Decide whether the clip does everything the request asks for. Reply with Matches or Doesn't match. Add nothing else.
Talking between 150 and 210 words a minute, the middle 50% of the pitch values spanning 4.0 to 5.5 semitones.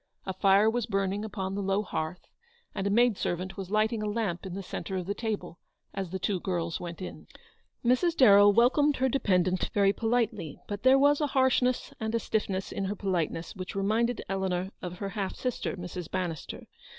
Doesn't match